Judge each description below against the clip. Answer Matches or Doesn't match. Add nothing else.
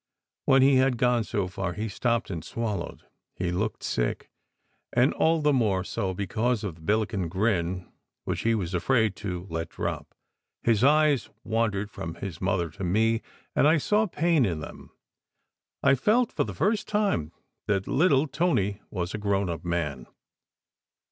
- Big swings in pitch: Matches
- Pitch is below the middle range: Matches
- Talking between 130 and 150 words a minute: Doesn't match